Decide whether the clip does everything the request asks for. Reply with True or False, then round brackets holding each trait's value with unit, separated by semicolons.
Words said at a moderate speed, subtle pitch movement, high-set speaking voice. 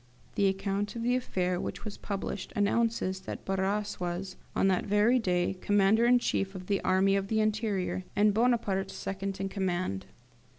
True (170 wpm; 1.9 semitones; 195 Hz)